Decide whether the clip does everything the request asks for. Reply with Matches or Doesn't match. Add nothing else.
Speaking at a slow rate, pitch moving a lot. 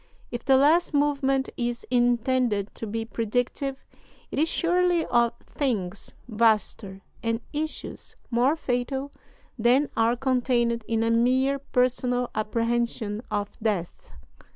Doesn't match